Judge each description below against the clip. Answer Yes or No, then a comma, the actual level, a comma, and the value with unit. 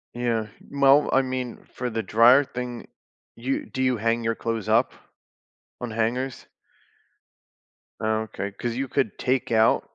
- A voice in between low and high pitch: No, low, 120 Hz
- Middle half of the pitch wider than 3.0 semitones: No, narrow, 2.4 semitones